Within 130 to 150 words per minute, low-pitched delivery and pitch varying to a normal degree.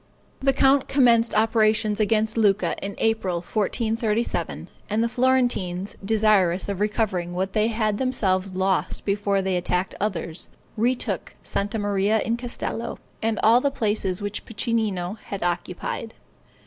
No: slow, 135 wpm; high, 215 Hz; average, 3.0 semitones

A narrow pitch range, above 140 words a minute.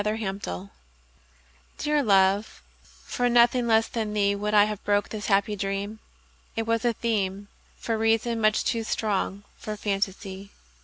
No: narrow, 2.1 semitones; slow, 135 wpm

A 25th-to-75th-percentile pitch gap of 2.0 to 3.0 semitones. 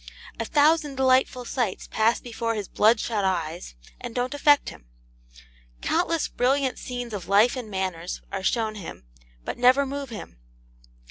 No: average, 4.8 semitones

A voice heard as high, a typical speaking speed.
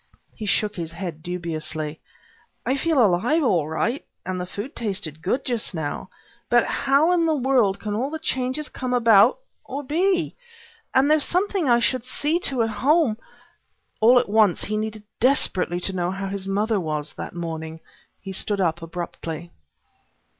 Yes: high, 215 Hz; average, 170 wpm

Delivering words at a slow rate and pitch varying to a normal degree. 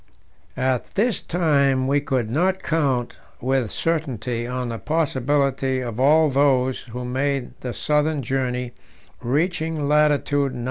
Yes: slow, 130 wpm; average, 3.1 semitones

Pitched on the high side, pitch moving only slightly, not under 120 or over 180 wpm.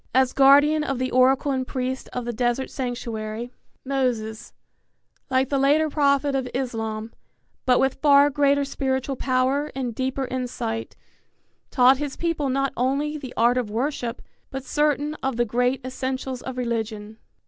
Yes: very high, 260 Hz; narrow, 2.2 semitones; average, 150 wpm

